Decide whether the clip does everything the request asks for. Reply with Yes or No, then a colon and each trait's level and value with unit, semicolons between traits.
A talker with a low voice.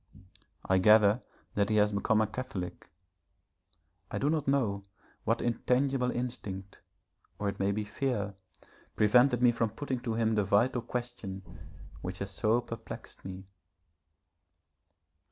Yes: low, 110 Hz